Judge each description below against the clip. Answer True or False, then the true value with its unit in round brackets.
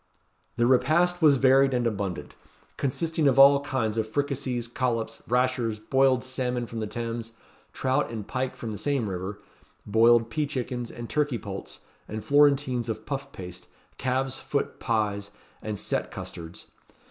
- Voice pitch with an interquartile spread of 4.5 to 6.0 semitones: False (3.5 semitones)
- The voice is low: True (125 Hz)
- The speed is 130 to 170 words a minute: True (155 wpm)